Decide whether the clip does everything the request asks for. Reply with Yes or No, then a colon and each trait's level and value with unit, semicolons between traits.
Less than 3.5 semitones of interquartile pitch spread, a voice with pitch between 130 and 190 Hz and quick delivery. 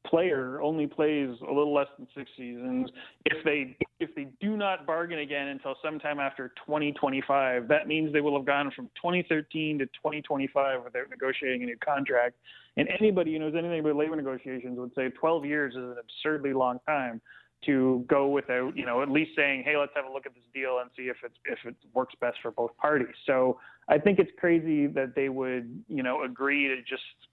Yes: average, 3.0 semitones; medium, 140 Hz; fast, 215 wpm